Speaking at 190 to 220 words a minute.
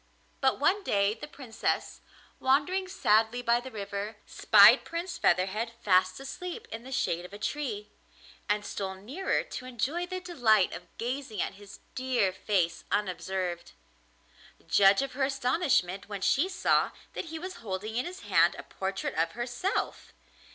No: average, 155 wpm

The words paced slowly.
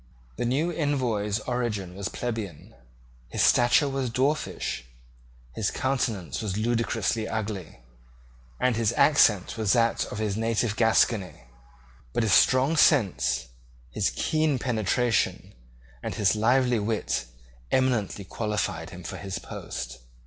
Yes: slow, 120 wpm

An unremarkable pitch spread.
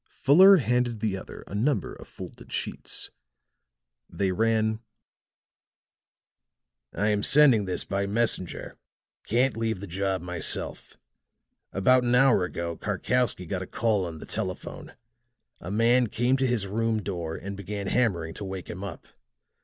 Yes: average, 4.1 semitones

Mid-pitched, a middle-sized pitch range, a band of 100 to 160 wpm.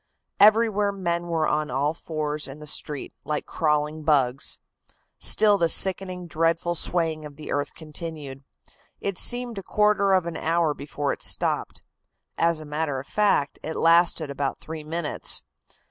Yes: medium, 160 Hz; average, 3.0 semitones; average, 155 wpm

